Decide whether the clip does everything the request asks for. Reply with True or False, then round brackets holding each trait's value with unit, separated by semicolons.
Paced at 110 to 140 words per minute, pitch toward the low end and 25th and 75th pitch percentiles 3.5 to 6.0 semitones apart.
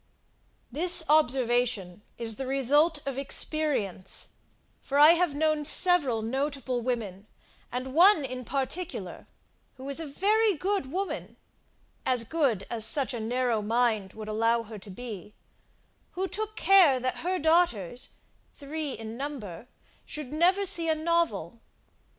False (135 wpm; 270 Hz; 5.6 semitones)